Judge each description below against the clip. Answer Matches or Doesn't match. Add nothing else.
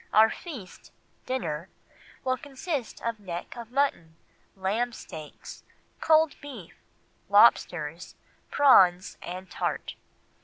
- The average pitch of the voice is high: Matches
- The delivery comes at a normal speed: Doesn't match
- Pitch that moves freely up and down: Matches